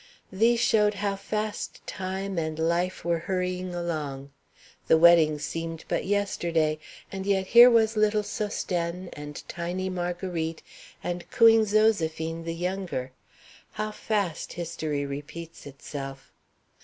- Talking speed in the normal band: No, slow, 120 wpm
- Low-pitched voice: No, medium, 175 Hz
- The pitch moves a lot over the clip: No, average, 3.8 semitones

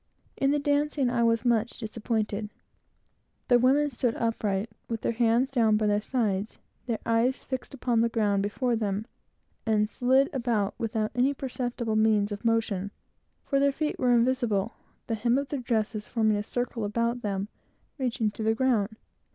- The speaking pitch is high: Yes, high, 230 Hz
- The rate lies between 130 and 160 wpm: No, average, 170 wpm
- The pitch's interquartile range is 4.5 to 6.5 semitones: No, average, 2.8 semitones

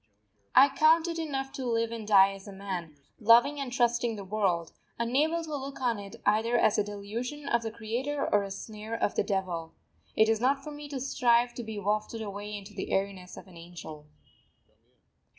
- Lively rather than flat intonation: No, average, 4.7 semitones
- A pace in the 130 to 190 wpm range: No, average, 200 wpm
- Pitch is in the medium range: No, high, 225 Hz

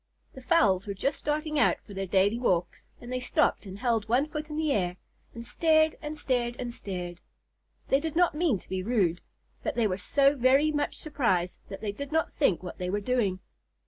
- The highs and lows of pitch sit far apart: Yes, wide, 7.4 semitones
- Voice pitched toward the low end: No, high, 240 Hz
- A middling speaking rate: No, fast, 210 wpm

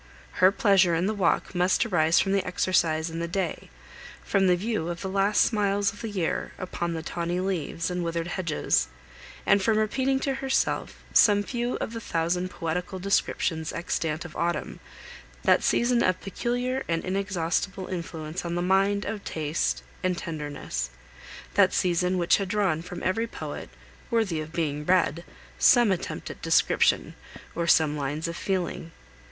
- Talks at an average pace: Yes, average, 165 wpm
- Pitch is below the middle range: No, medium, 180 Hz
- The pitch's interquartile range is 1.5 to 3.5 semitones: Yes, average, 3.2 semitones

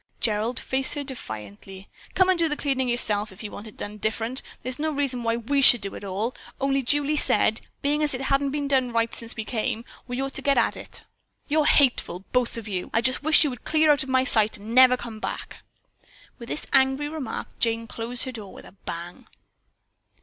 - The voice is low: No, very high, 250 Hz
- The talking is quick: Yes, fast, 225 wpm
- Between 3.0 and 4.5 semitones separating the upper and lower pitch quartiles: Yes, average, 4.1 semitones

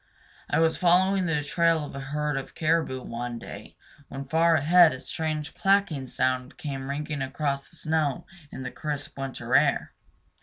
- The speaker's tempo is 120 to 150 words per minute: No, average, 165 wpm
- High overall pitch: No, medium, 150 Hz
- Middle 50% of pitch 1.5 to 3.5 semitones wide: Yes, average, 3.2 semitones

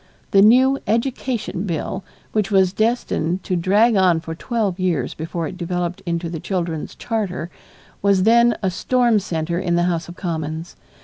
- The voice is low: No, medium, 185 Hz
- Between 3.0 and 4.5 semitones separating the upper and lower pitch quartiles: Yes, average, 4.1 semitones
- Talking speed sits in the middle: Yes, average, 165 wpm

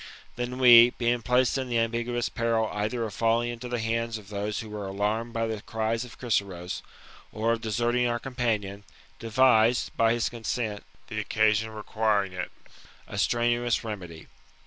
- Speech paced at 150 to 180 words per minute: Yes, average, 170 wpm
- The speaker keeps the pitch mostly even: Yes, narrow, 1.9 semitones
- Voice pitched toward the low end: Yes, low, 115 Hz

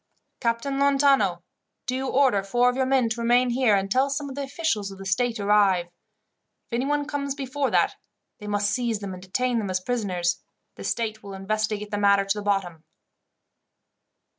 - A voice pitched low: No, high, 220 Hz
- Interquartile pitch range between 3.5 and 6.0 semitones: Yes, average, 4.8 semitones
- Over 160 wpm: Yes, average, 185 wpm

